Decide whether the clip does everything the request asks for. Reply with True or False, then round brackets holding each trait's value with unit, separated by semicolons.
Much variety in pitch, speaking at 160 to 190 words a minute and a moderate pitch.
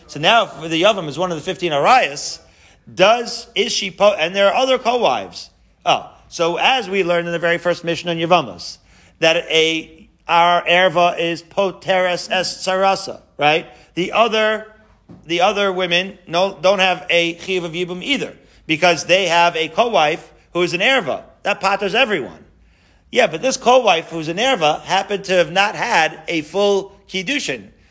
False (2.8 semitones; 170 wpm; 180 Hz)